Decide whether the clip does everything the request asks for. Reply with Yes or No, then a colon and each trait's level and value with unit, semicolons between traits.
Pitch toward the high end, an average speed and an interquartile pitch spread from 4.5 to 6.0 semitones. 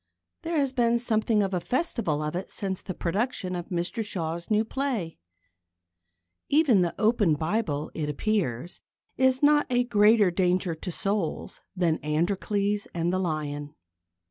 Yes: high, 195 Hz; average, 145 wpm; wide, 5.4 semitones